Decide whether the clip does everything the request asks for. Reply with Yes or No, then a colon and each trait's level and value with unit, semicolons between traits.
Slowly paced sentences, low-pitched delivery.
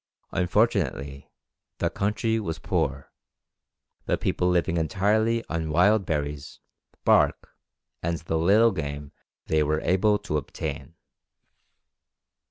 Yes: slow, 105 wpm; very low, 85 Hz